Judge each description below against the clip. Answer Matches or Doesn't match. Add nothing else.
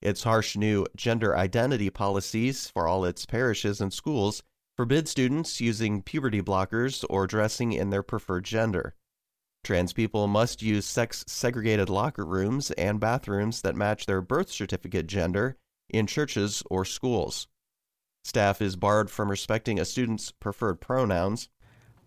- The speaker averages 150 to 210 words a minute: Doesn't match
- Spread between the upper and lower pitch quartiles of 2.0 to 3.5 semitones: Matches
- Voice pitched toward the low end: Matches